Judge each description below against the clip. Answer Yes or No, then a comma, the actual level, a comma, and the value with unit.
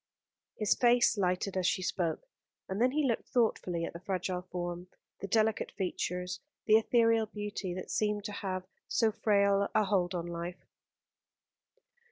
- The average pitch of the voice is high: Yes, high, 195 Hz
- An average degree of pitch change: Yes, average, 3.3 semitones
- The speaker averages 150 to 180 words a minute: Yes, average, 155 wpm